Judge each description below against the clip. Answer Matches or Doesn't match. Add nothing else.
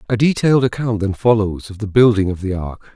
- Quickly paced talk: Matches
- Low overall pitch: Matches